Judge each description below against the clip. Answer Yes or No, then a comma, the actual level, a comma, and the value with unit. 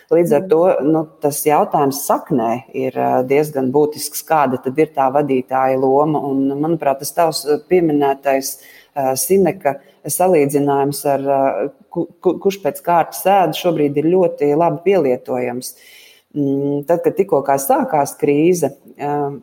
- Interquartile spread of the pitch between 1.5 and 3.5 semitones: Yes, average, 3.1 semitones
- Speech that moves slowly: Yes, slow, 105 wpm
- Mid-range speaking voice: Yes, medium, 145 Hz